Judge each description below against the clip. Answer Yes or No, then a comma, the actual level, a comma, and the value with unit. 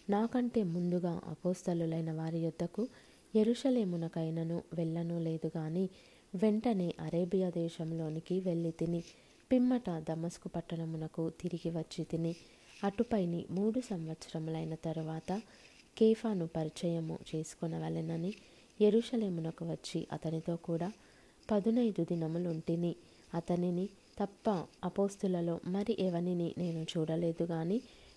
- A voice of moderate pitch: Yes, medium, 170 Hz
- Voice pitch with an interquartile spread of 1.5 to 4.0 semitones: Yes, average, 3.0 semitones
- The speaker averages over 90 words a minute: No, average, 85 wpm